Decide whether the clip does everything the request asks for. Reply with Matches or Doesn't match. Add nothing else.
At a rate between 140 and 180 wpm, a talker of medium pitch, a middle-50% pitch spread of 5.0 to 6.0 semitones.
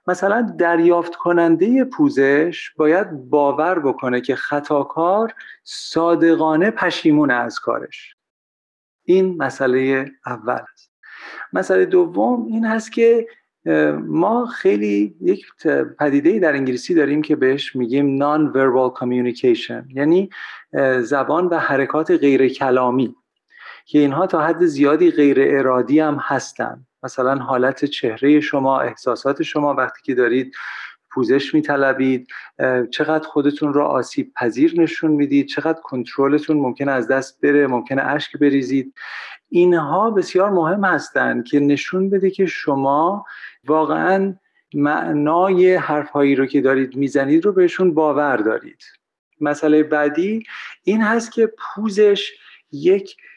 Doesn't match